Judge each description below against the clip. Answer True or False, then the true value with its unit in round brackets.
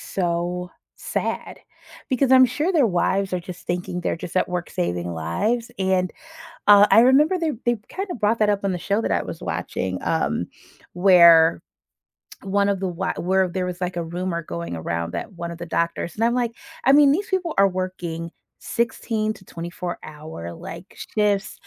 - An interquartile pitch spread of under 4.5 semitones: False (4.8 semitones)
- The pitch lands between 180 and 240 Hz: True (185 Hz)